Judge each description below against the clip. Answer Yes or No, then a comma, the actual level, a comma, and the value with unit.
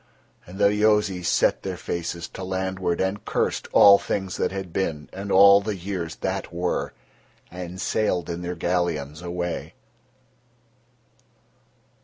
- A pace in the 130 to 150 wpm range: Yes, slow, 135 wpm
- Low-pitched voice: Yes, very low, 90 Hz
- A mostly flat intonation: Yes, narrow, 2.1 semitones